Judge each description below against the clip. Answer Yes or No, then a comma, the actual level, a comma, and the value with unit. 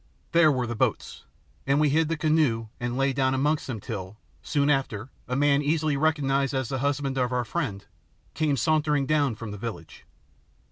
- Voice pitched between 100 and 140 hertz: Yes, low, 135 Hz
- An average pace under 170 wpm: No, average, 185 wpm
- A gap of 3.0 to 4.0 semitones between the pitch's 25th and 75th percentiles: Yes, average, 3.6 semitones